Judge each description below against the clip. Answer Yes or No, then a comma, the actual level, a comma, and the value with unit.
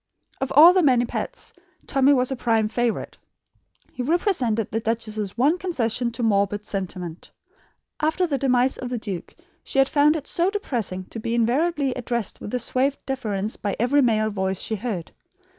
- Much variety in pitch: No, average, 4.3 semitones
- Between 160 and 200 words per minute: Yes, average, 165 wpm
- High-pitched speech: Yes, high, 240 Hz